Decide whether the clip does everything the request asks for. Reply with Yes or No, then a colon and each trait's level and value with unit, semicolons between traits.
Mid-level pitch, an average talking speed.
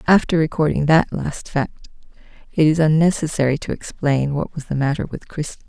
Yes: medium, 150 Hz; average, 170 wpm